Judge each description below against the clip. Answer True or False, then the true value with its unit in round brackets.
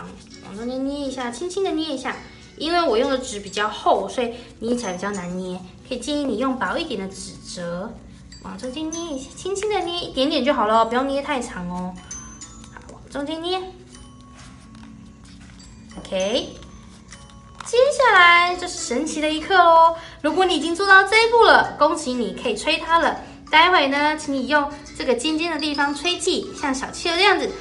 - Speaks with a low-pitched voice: False (295 Hz)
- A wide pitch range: True (5.7 semitones)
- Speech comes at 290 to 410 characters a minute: False (265 characters per minute)